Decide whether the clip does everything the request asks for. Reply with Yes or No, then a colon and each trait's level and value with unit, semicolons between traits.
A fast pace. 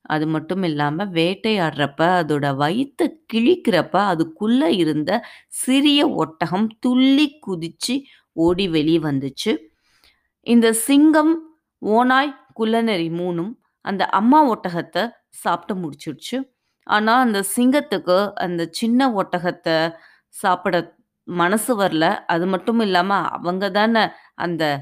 No: average, 100 wpm